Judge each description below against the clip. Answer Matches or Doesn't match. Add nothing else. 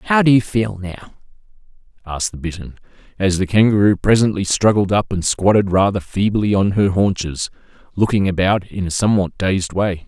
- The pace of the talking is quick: Doesn't match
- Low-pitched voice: Matches